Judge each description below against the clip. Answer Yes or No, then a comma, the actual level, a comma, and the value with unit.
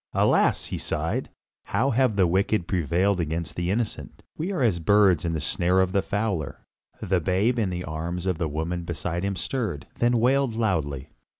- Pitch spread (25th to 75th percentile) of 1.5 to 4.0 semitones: No, average, 4.4 semitones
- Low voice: Yes, very low, 90 Hz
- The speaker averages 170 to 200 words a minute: Yes, average, 185 wpm